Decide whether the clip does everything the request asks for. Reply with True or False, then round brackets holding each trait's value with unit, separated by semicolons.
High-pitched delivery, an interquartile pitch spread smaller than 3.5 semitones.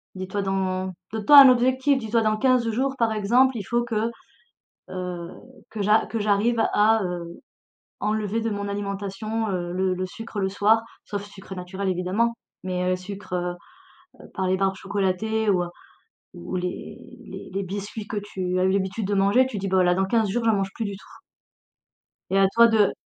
True (200 Hz; 3.0 semitones)